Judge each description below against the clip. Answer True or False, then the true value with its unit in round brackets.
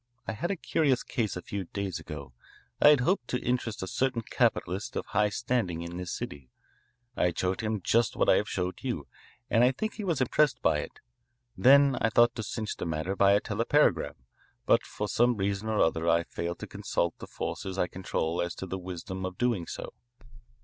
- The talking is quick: True (210 wpm)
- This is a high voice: False (100 Hz)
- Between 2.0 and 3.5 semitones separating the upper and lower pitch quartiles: False (5.5 semitones)